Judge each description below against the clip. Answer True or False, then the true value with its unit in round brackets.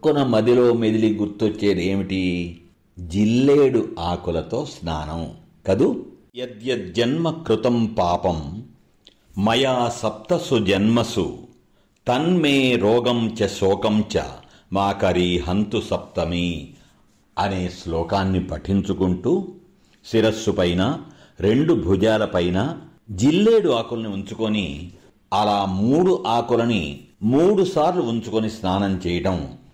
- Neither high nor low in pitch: False (105 Hz)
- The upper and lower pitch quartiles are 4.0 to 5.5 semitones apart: True (4.7 semitones)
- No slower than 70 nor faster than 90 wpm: True (80 wpm)